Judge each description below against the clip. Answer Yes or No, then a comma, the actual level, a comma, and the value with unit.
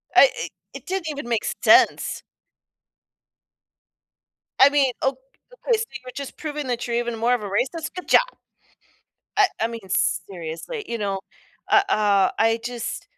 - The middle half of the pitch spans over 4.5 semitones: Yes, average, 5.2 semitones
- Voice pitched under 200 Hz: No, high, 245 Hz